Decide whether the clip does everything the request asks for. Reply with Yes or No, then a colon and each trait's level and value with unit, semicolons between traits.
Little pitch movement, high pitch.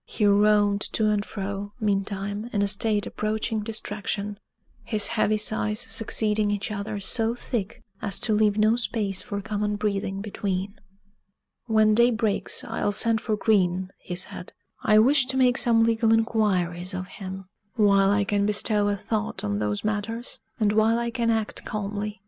Yes: narrow, 1.6 semitones; high, 210 Hz